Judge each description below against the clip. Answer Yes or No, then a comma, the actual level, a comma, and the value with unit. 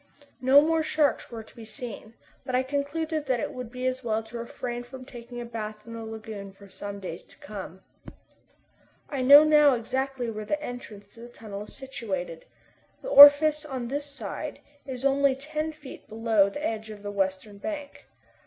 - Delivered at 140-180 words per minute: No, average, 190 wpm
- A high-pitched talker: Yes, high, 245 Hz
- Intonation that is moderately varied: Yes, average, 4.6 semitones